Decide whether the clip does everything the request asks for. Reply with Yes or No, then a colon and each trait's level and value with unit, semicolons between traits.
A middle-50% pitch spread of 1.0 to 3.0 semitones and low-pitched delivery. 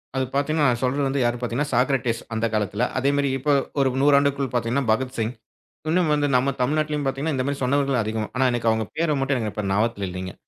No: average, 3.5 semitones; low, 130 Hz